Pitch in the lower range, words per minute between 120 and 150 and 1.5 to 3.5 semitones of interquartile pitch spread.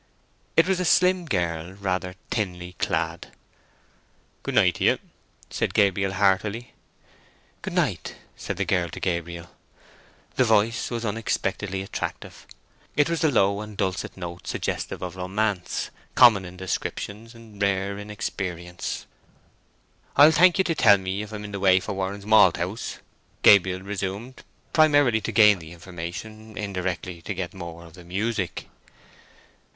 Yes: low, 100 Hz; average, 145 wpm; average, 3.2 semitones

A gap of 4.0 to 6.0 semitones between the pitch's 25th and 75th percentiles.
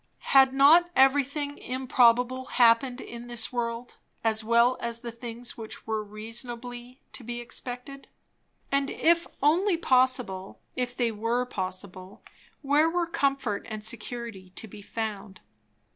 No: average, 3.0 semitones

